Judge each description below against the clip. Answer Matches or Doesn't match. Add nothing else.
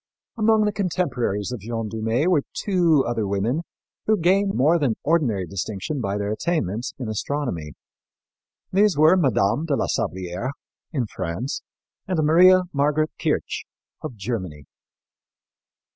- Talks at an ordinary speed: Doesn't match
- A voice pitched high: Doesn't match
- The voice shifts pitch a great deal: Matches